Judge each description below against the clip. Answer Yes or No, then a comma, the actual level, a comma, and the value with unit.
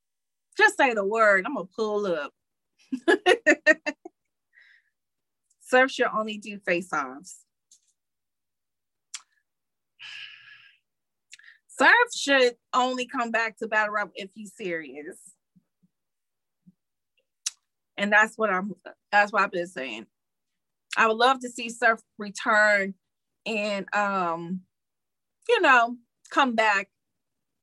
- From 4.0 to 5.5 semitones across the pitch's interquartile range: Yes, average, 4.6 semitones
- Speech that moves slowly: Yes, slow, 100 wpm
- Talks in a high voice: Yes, high, 220 Hz